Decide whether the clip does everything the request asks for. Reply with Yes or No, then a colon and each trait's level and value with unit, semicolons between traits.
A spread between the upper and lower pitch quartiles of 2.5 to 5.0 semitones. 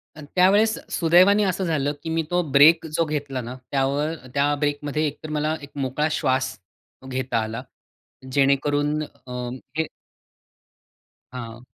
Yes: average, 3.1 semitones